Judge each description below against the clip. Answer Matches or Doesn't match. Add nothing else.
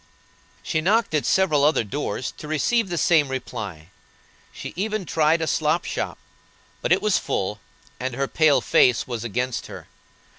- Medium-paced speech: Matches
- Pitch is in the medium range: Matches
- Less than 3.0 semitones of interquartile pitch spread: Doesn't match